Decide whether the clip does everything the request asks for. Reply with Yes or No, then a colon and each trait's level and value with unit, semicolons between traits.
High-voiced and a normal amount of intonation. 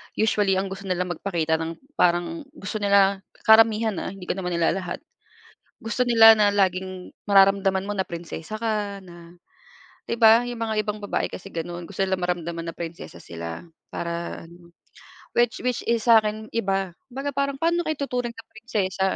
Yes: high, 195 Hz; average, 4.0 semitones